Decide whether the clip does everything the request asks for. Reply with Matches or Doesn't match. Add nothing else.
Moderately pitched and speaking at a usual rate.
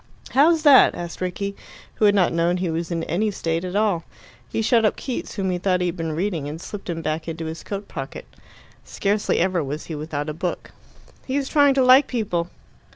Doesn't match